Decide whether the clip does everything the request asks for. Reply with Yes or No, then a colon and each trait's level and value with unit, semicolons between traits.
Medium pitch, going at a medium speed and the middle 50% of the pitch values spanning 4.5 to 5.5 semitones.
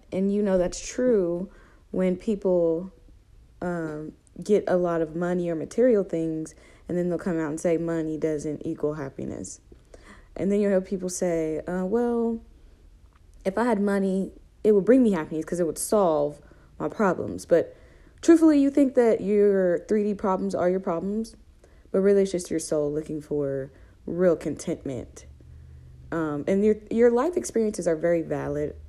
Yes: medium, 175 Hz; average, 165 wpm; average, 4.8 semitones